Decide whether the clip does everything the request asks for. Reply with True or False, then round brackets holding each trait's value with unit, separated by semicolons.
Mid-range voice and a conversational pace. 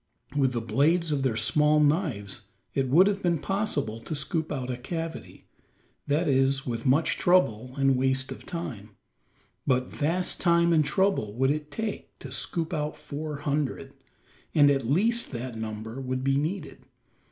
True (145 Hz; 165 wpm)